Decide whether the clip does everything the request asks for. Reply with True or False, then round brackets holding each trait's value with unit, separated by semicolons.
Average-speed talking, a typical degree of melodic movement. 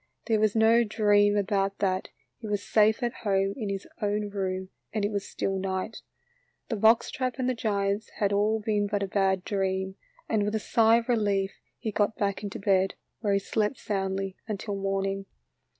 False (185 wpm; 1.9 semitones)